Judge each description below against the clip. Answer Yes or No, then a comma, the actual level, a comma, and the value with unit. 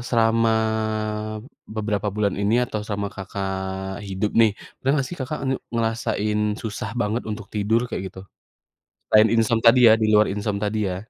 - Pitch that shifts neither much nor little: No, narrow, 2.1 semitones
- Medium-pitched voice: No, low, 105 Hz